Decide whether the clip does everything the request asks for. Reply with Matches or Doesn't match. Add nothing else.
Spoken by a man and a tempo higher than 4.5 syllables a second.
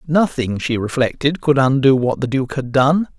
Matches